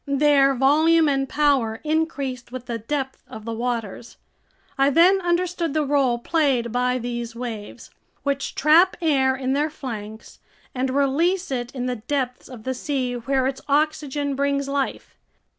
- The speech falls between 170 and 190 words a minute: No, average, 155 wpm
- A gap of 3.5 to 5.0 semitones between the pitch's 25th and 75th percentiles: No, average, 3.1 semitones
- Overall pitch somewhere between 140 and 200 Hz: No, very high, 270 Hz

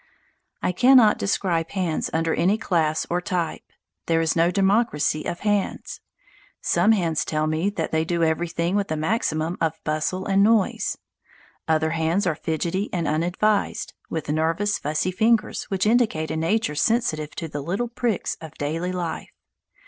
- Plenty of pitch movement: No, average, 4.0 semitones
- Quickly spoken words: No, average, 155 wpm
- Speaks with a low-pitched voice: No, medium, 170 Hz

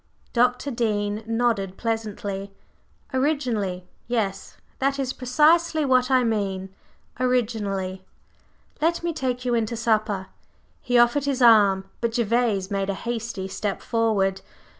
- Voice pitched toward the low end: No, high, 230 Hz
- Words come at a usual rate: No, slow, 125 wpm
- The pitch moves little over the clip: No, average, 4.0 semitones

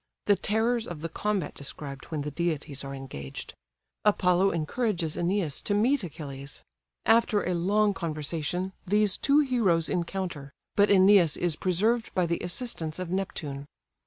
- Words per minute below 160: Yes, average, 145 wpm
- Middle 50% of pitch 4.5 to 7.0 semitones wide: Yes, average, 5.1 semitones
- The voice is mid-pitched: Yes, medium, 180 Hz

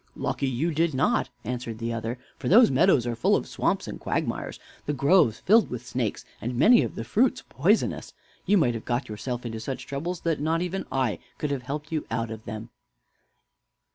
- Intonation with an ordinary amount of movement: No, wide, 5.9 semitones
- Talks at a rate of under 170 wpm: No, average, 200 wpm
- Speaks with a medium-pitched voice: No, low, 130 Hz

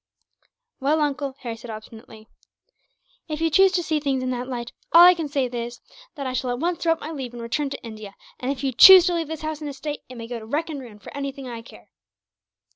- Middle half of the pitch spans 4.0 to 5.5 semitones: Yes, average, 4.4 semitones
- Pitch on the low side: No, very high, 270 Hz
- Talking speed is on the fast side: Yes, fast, 250 wpm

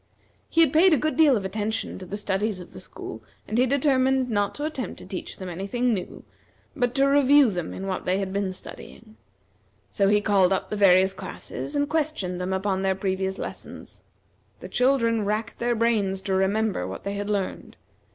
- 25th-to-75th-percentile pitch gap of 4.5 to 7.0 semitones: Yes, average, 4.9 semitones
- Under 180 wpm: No, average, 200 wpm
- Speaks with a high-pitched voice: Yes, high, 210 Hz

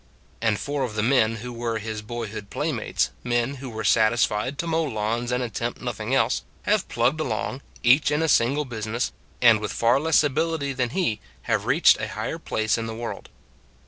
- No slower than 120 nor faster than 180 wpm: No, average, 195 wpm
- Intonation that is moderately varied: Yes, average, 3.8 semitones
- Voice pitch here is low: Yes, low, 120 Hz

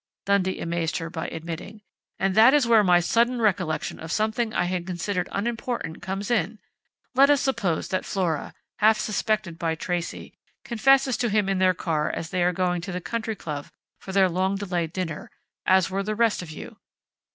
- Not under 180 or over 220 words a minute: Yes, average, 190 wpm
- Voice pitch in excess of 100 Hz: Yes, high, 190 Hz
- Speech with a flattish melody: No, average, 4.1 semitones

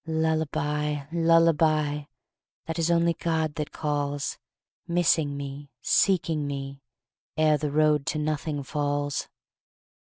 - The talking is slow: Yes, slow, 110 wpm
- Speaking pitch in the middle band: Yes, medium, 150 Hz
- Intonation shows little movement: Yes, narrow, 1.9 semitones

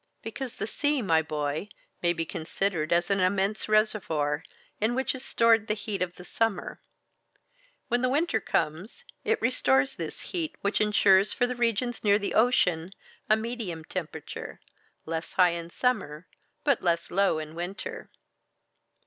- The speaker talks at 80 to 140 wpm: No, average, 150 wpm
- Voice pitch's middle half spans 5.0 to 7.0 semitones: Yes, wide, 5.5 semitones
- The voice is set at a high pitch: Yes, high, 200 Hz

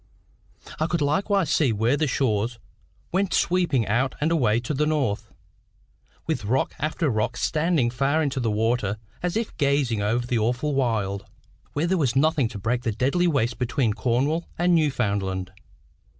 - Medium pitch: No, low, 130 Hz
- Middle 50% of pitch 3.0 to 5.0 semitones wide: No, wide, 5.4 semitones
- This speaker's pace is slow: No, average, 165 wpm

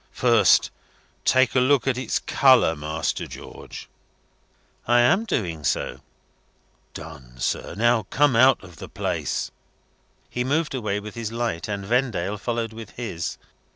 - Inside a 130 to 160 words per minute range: Yes, average, 140 wpm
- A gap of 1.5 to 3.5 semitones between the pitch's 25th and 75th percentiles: No, average, 5.3 semitones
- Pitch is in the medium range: No, low, 115 Hz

